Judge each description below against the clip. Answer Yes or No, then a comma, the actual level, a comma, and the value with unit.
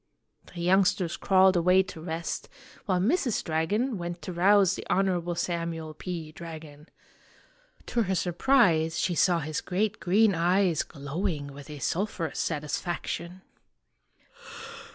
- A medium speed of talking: No, slow, 125 wpm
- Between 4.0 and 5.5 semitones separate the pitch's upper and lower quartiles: No, average, 2.8 semitones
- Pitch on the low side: No, medium, 175 Hz